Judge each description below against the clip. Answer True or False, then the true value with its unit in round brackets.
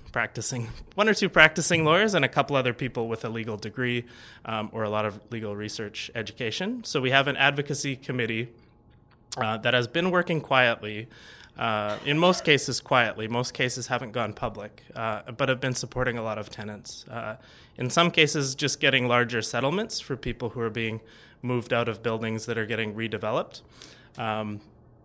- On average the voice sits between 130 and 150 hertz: False (120 Hz)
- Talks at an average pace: True (180 wpm)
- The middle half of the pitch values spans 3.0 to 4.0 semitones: True (3.3 semitones)